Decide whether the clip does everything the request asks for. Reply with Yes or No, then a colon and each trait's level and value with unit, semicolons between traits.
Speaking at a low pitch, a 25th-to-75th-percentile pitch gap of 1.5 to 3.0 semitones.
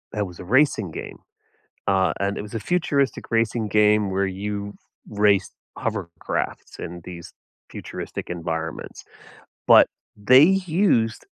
No: low, 105 Hz; average, 3.6 semitones